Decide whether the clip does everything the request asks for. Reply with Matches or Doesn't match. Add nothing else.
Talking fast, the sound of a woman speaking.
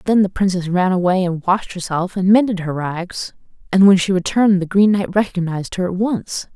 Matches